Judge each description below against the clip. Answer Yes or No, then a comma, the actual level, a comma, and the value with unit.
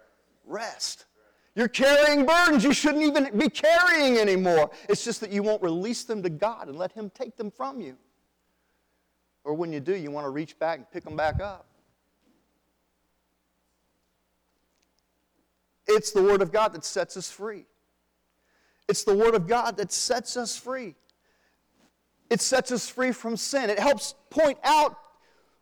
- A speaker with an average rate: Yes, average, 160 wpm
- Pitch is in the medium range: No, high, 205 Hz